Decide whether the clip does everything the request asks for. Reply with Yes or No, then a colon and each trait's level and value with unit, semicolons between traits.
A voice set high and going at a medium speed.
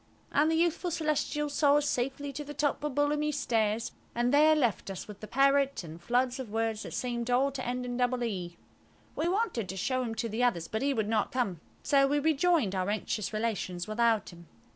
No: high, 245 Hz; fast, 215 wpm